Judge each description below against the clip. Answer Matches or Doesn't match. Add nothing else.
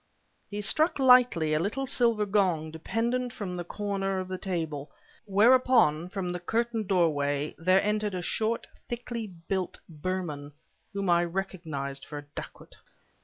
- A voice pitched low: Doesn't match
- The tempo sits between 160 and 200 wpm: Doesn't match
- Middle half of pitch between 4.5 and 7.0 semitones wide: Matches